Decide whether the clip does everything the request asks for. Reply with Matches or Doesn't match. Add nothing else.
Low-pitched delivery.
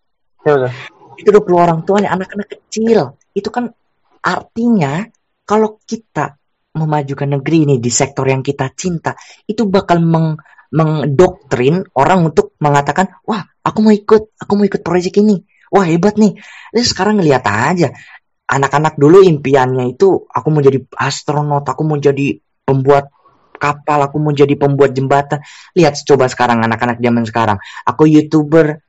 Doesn't match